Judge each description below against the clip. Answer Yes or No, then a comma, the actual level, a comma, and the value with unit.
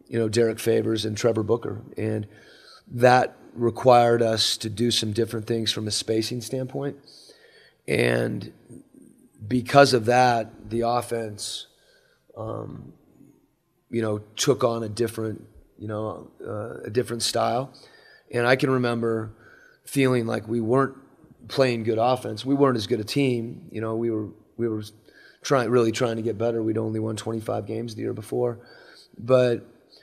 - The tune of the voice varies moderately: No, narrow, 1.9 semitones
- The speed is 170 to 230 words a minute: No, average, 155 wpm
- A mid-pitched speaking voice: No, low, 115 Hz